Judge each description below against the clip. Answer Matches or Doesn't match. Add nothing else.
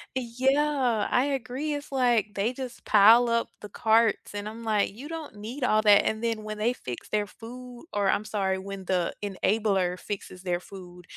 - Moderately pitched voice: Doesn't match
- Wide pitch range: Doesn't match